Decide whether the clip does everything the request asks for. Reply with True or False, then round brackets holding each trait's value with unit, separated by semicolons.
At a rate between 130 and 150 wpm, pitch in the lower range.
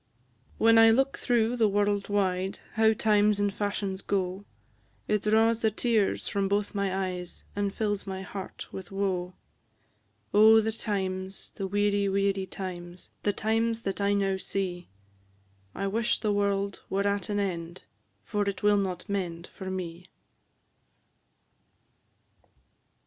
False (140 wpm; 200 Hz)